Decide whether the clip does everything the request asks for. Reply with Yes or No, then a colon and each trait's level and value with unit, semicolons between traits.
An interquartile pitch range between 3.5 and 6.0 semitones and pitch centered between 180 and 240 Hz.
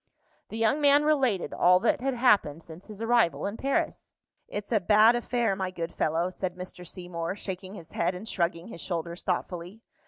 Yes: average, 4.6 semitones; high, 190 Hz